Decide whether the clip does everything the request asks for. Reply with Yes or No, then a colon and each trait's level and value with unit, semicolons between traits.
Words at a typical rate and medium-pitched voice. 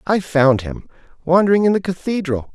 Yes: average, 165 wpm; medium, 170 Hz